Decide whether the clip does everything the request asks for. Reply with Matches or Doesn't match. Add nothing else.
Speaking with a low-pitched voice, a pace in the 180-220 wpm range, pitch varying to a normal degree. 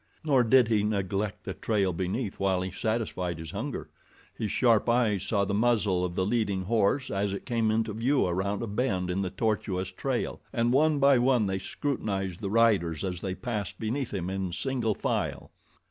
Matches